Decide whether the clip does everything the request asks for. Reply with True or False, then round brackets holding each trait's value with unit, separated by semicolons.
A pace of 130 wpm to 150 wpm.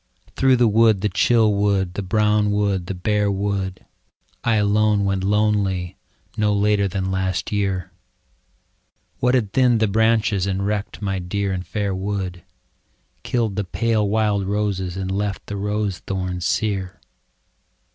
True (145 wpm)